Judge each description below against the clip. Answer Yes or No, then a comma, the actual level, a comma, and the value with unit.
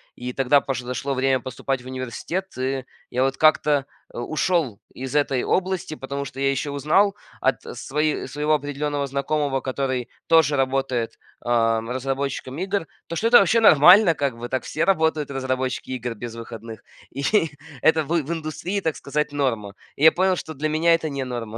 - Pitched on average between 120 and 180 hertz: Yes, medium, 140 Hz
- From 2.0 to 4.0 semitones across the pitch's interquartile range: Yes, average, 3.3 semitones